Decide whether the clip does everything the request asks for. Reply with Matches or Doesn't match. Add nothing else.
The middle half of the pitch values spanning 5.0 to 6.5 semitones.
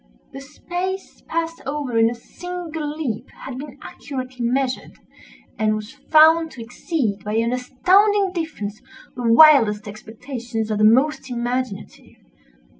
Matches